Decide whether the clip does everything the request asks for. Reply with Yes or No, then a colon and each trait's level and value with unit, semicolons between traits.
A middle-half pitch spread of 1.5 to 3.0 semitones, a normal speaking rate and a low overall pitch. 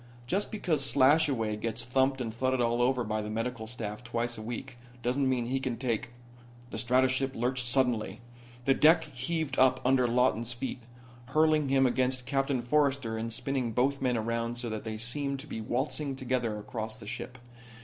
Yes: narrow, 2.4 semitones; average, 180 wpm; low, 125 Hz